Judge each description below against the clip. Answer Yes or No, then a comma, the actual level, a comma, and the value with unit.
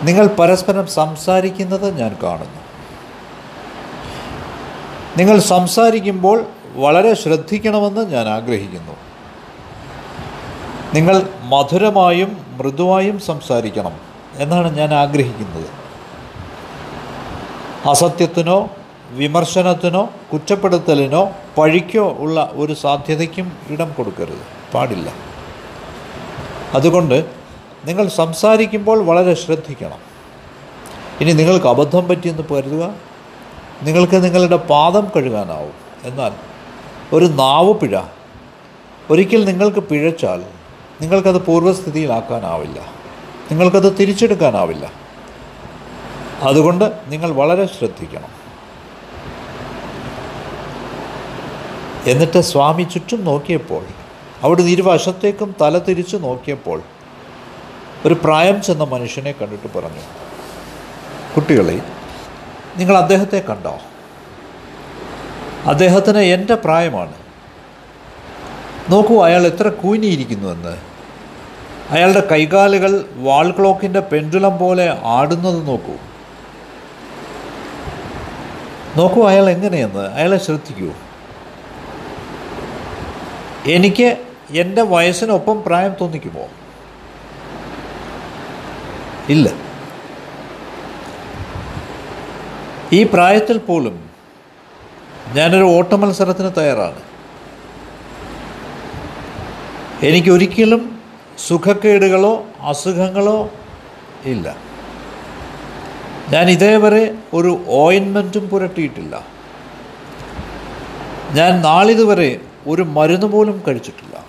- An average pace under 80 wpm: Yes, average, 65 wpm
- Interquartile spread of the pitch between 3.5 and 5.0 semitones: Yes, average, 4.4 semitones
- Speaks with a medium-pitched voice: Yes, medium, 180 Hz